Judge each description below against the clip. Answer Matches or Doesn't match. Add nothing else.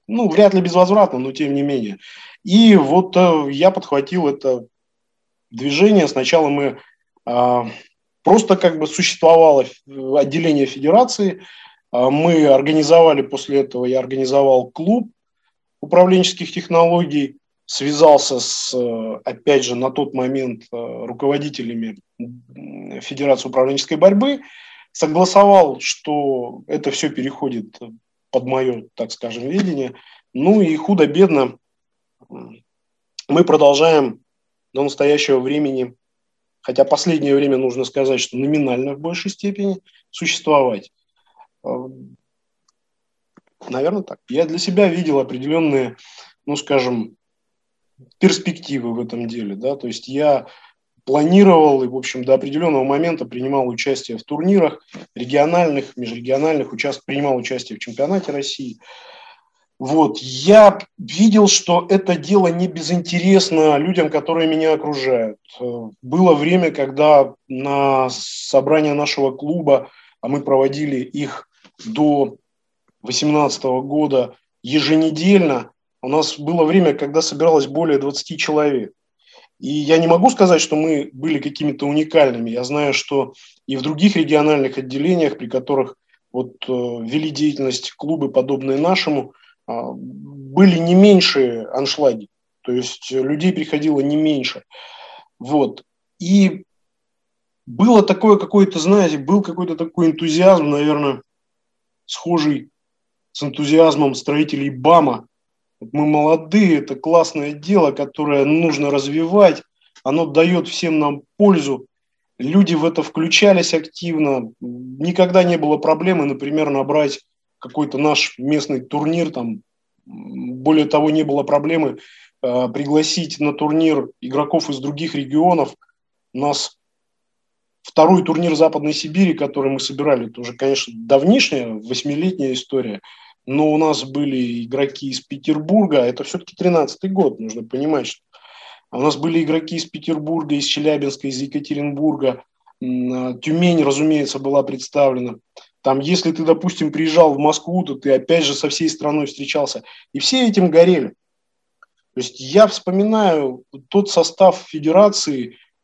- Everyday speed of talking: Matches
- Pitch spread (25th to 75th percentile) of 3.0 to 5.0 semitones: Matches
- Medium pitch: Matches